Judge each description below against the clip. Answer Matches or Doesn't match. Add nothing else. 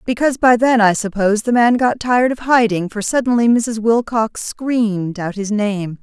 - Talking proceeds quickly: Doesn't match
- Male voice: Doesn't match